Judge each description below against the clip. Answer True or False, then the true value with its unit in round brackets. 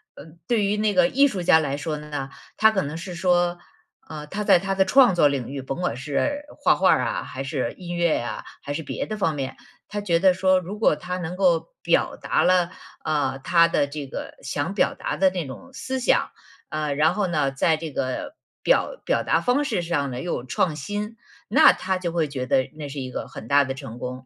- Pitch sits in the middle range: True (170 Hz)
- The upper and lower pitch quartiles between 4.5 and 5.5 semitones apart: True (5.2 semitones)